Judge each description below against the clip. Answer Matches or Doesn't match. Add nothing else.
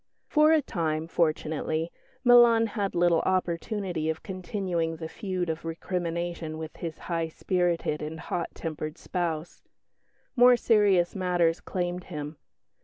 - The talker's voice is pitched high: Doesn't match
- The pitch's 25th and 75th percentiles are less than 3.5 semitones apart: Matches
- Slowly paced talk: Matches